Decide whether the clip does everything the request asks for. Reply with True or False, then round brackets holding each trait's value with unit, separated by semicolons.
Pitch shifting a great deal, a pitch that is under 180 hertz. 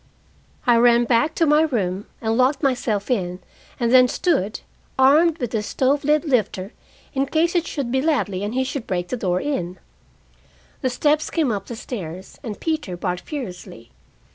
False (6.3 semitones; 245 Hz)